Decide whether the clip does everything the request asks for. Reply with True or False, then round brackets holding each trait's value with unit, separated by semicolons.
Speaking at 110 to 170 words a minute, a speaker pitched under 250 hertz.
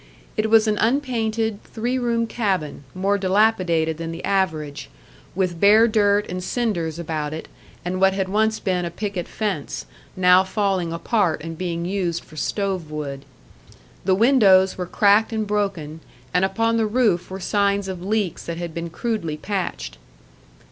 True (160 wpm; 190 Hz)